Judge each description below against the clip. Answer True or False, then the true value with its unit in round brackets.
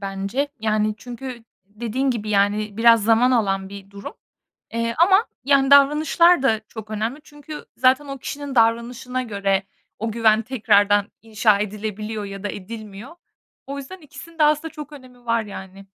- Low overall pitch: False (230 Hz)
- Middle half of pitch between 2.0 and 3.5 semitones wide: False (4.5 semitones)